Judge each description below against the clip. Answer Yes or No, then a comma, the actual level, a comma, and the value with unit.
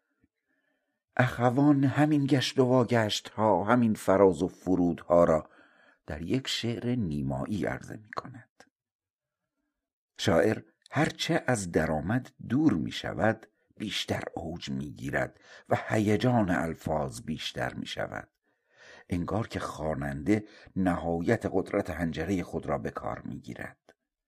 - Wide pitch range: Yes, wide, 6.5 semitones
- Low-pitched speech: Yes, low, 105 Hz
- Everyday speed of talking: Yes, average, 120 wpm